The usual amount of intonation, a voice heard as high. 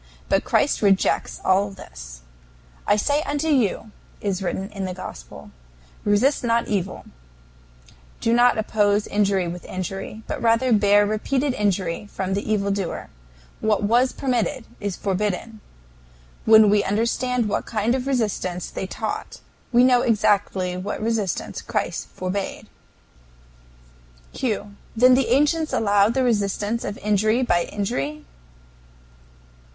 Yes: average, 3.2 semitones; high, 210 Hz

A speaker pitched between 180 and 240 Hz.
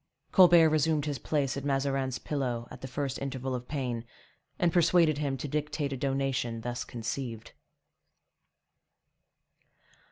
No: low, 135 Hz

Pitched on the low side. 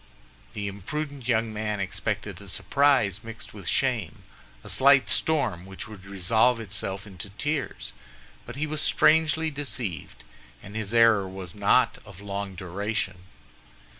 Yes: low, 105 Hz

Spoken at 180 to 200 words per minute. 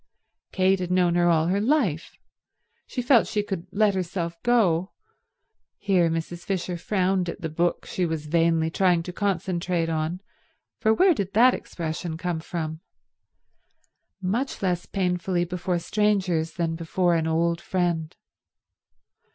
No: slow, 135 wpm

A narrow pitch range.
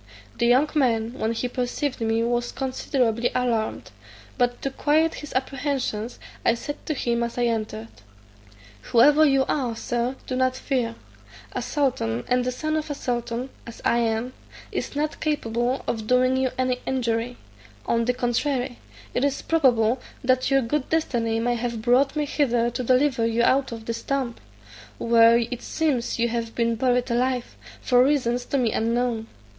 Yes: narrow, 2.3 semitones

